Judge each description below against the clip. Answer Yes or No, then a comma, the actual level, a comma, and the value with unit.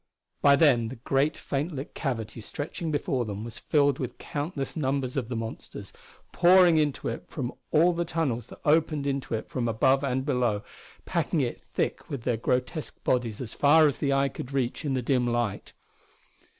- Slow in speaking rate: No, average, 185 wpm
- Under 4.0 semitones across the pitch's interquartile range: Yes, average, 3.5 semitones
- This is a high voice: No, low, 135 Hz